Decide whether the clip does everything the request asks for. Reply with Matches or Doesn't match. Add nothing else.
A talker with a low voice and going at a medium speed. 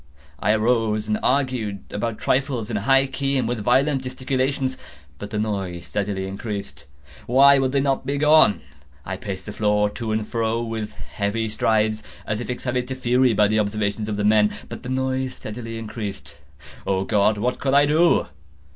Matches